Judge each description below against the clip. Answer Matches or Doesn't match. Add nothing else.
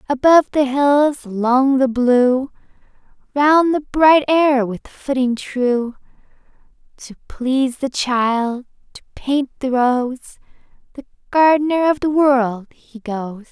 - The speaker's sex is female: Matches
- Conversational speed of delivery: Doesn't match